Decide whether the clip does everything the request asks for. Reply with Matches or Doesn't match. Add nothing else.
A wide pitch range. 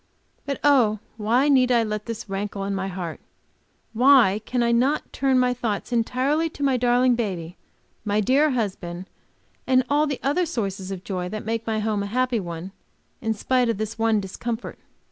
Doesn't match